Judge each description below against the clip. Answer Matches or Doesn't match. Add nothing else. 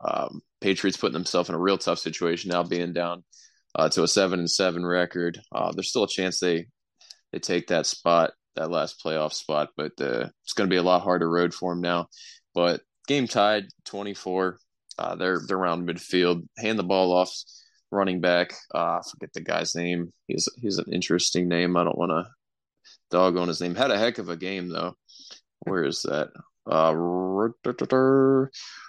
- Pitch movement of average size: Doesn't match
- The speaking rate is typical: Matches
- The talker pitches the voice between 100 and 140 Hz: Doesn't match